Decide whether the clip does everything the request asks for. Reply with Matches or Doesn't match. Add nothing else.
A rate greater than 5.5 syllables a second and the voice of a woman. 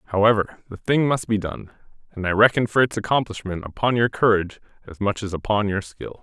Doesn't match